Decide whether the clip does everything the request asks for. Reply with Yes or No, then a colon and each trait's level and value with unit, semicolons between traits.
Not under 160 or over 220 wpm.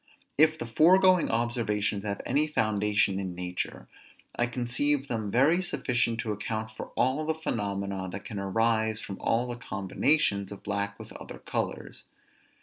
No: average, 150 wpm